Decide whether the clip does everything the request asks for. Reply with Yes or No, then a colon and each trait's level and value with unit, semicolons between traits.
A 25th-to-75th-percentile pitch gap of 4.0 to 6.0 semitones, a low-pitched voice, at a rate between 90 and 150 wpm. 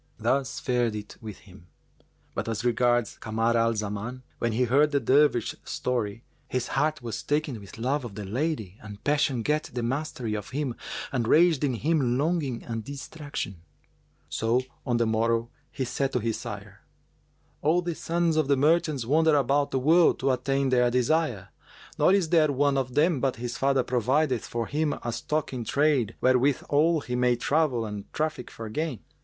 No: average, 4.3 semitones; low, 130 Hz; average, 180 wpm